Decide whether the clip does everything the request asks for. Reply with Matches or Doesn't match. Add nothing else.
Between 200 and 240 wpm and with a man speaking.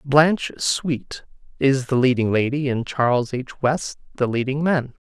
Doesn't match